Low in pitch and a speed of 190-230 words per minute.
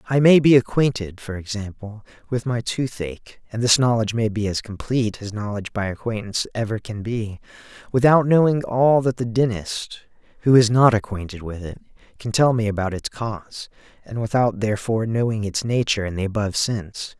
No: low, 110 Hz; average, 180 wpm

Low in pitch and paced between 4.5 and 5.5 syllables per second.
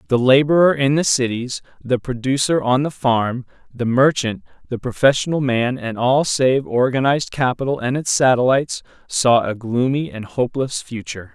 Yes: low, 130 Hz; 5.0 syllables/s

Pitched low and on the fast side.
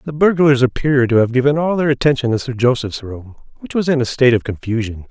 Yes: low, 130 Hz; fast, 235 wpm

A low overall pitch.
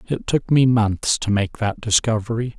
Yes: low, 115 Hz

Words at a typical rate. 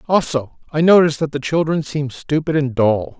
Yes: average, 190 wpm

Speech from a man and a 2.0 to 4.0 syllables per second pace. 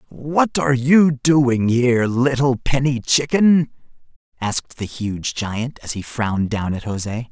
Yes: male; 3.9 syllables/s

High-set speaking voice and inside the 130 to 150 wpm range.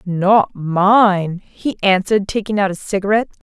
Yes: high, 195 Hz; slow, 135 wpm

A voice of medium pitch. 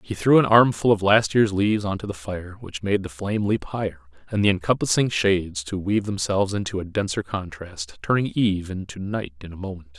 No: very low, 95 Hz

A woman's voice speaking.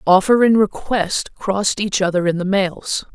Yes: female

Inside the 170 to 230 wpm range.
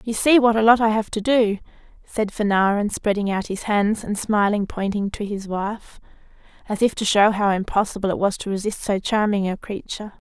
Yes: fast, 205 wpm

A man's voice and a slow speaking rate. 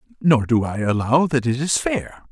No: male; fast, 205 wpm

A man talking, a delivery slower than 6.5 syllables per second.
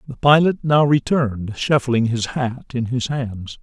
Yes: male; 4.2 syllables/s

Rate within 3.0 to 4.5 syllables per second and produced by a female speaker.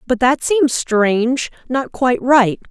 Yes: 3.9 syllables/s; female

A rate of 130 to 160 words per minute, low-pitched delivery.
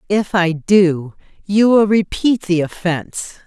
No: average, 140 wpm; high, 190 Hz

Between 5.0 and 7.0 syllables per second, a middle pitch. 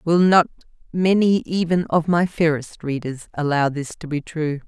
No: 4.4 syllables/s; medium, 160 Hz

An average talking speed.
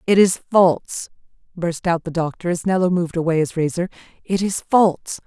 Yes: average, 180 wpm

